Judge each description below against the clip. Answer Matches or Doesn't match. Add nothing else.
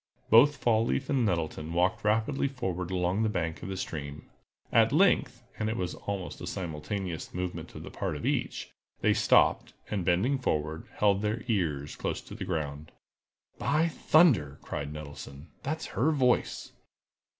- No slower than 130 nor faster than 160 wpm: Matches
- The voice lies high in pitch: Doesn't match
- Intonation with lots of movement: Matches